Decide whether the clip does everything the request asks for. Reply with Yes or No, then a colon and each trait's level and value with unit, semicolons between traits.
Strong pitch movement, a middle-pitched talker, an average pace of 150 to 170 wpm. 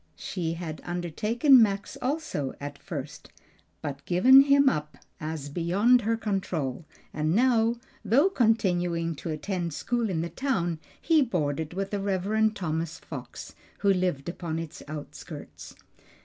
No: wide, 5.8 semitones; medium, 180 Hz; slow, 135 wpm